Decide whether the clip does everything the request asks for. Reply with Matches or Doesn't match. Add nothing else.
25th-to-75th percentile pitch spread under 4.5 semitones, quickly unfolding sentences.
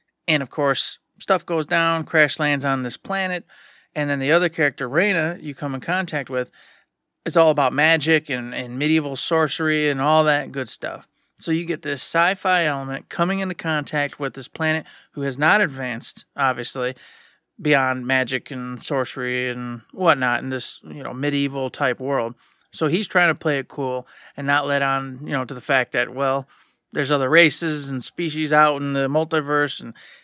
Doesn't match